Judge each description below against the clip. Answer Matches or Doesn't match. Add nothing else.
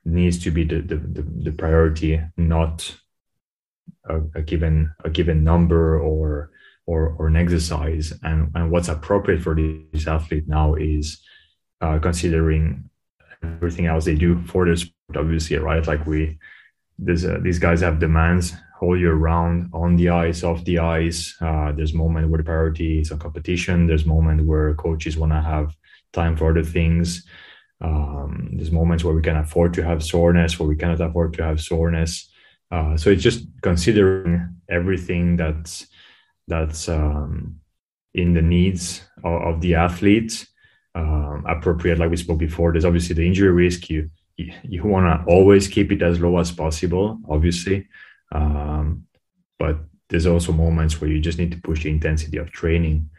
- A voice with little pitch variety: Matches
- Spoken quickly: Doesn't match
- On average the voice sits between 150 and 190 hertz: Doesn't match